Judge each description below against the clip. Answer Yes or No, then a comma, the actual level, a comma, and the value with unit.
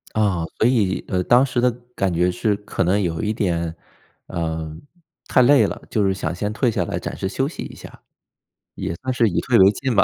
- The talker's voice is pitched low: Yes, low, 100 Hz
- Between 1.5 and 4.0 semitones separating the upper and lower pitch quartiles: No, average, 5.0 semitones